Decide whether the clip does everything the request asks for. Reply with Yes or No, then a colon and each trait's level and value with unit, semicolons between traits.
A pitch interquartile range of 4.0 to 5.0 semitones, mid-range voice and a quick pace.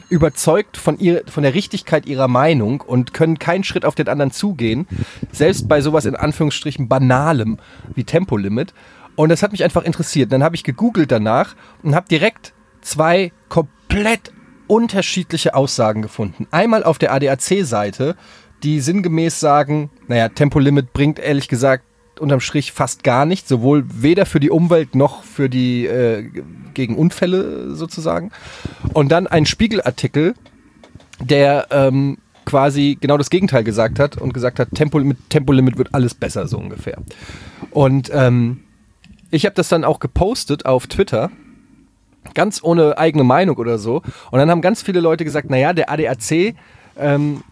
No: average, 4.3 semitones; medium, 150 Hz; average, 155 wpm